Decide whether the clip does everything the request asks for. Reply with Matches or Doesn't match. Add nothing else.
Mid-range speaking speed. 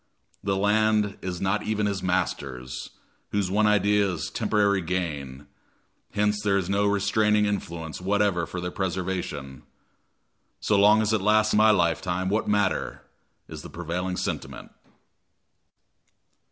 Doesn't match